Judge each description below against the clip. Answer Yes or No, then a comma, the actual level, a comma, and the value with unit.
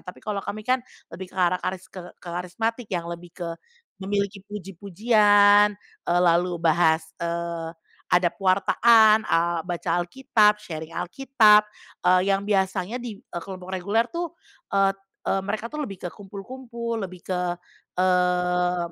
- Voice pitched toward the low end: No, high, 190 Hz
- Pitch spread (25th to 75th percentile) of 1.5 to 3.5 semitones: Yes, average, 3.0 semitones